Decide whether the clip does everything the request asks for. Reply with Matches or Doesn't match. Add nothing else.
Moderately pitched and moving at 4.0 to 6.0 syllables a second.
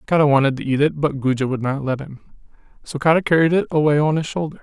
Doesn't match